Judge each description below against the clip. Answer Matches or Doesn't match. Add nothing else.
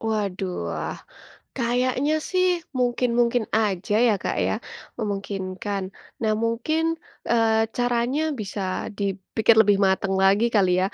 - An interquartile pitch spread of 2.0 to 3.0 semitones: Doesn't match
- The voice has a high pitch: Matches